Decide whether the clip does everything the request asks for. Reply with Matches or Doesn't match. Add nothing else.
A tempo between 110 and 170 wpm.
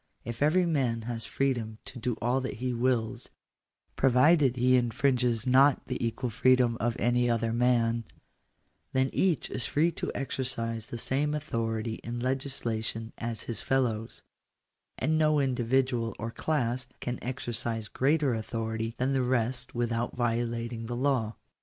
Matches